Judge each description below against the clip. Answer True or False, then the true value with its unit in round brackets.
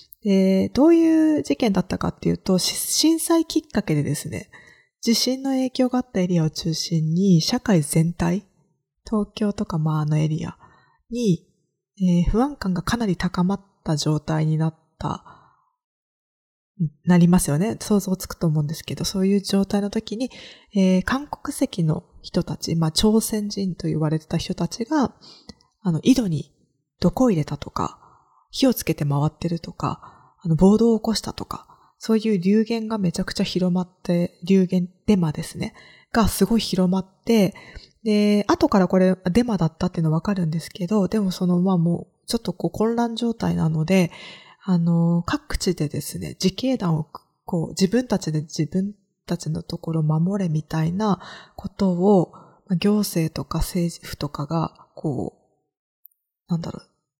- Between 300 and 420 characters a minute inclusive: True (305 characters per minute)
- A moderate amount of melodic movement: True (4.4 semitones)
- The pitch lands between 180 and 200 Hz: True (185 Hz)